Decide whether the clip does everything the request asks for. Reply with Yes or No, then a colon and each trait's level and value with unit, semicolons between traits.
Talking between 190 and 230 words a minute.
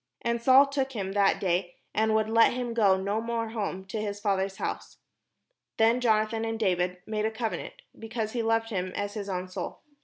Yes: average, 195 wpm